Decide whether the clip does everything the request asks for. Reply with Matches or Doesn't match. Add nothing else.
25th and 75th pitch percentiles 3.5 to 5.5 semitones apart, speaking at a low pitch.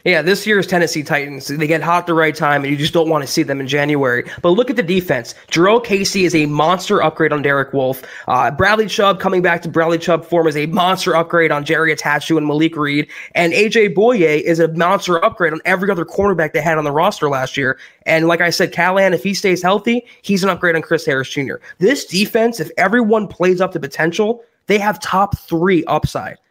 Doesn't match